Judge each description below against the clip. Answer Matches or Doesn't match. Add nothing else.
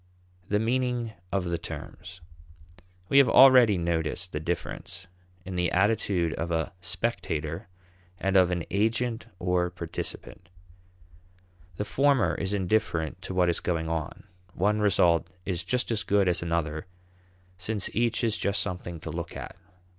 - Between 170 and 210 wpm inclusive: Doesn't match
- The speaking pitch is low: Matches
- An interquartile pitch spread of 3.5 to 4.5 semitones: Matches